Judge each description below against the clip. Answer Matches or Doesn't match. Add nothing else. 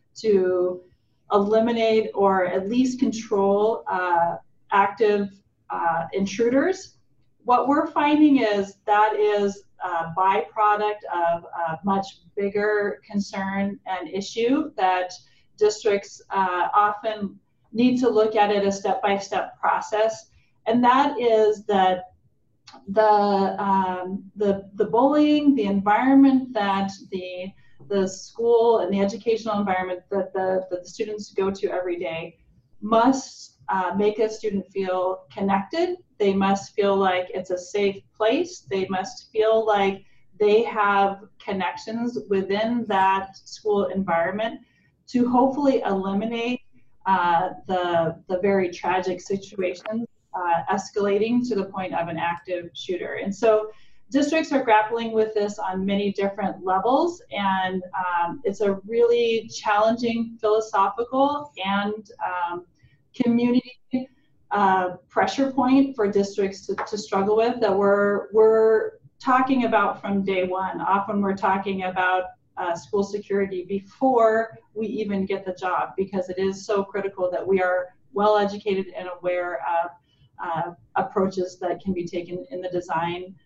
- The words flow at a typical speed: Doesn't match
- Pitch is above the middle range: Matches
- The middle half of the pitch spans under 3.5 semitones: Matches